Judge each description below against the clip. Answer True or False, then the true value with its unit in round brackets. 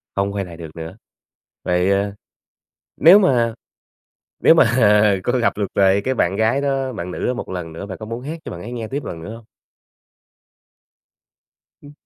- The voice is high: False (105 Hz)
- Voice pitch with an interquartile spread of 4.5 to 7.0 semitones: True (5.0 semitones)